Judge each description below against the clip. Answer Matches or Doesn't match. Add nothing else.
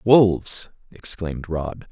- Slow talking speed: Matches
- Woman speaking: Doesn't match